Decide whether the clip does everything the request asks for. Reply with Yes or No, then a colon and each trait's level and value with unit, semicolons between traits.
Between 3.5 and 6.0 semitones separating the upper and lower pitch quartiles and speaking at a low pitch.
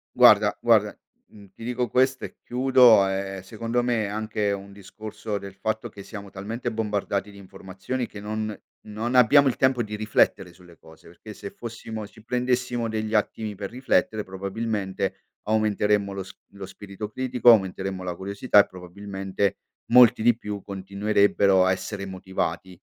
No: average, 2.8 semitones; low, 105 Hz